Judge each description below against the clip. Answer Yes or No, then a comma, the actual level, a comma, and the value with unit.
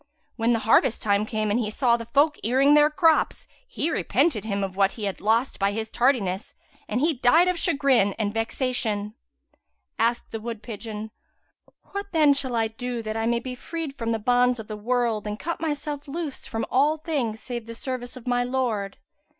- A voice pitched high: Yes, high, 240 Hz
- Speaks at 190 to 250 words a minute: Yes, average, 195 wpm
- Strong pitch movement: No, average, 4.0 semitones